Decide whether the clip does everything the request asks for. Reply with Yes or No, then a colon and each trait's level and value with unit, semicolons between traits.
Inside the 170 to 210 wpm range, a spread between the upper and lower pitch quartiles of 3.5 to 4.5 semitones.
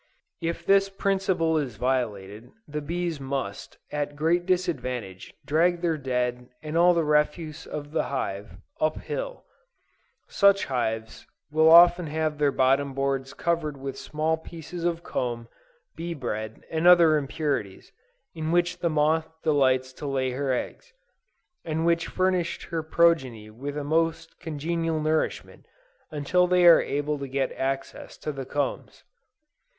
No: average, 145 wpm; average, 3.9 semitones